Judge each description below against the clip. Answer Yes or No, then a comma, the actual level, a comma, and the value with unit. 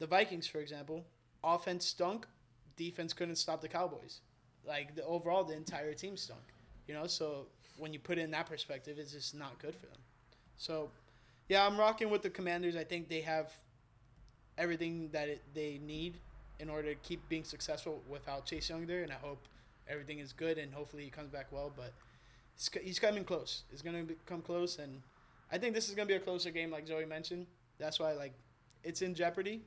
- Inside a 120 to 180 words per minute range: No, fast, 205 wpm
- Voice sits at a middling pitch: Yes, medium, 155 Hz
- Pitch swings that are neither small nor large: Yes, average, 3.6 semitones